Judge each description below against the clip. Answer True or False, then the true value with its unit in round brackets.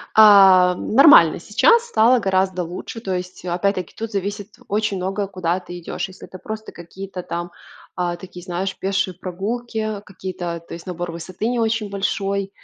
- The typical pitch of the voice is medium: False (195 Hz)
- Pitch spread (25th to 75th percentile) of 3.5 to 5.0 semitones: False (2.8 semitones)